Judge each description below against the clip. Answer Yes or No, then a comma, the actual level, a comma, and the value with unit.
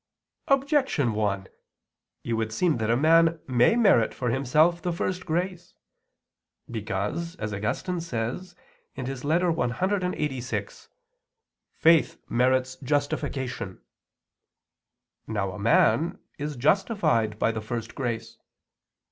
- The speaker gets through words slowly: Yes, slow, 105 wpm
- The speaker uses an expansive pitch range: Yes, wide, 6.9 semitones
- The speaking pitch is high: No, low, 135 Hz